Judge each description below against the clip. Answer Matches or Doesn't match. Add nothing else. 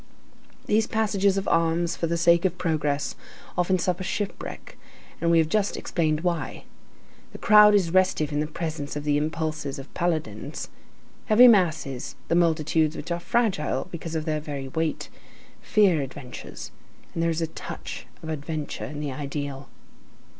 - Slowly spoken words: Doesn't match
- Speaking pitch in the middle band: Matches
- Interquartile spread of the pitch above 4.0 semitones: Doesn't match